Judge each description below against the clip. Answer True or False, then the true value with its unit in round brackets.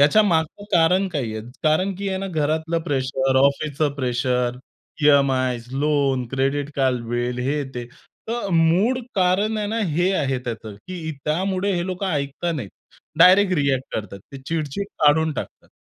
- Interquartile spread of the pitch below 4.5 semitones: False (5.5 semitones)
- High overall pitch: False (150 Hz)